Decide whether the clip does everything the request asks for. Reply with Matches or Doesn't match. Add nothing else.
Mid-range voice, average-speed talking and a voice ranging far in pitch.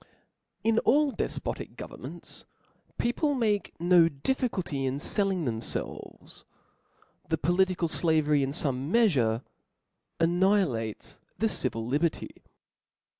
Doesn't match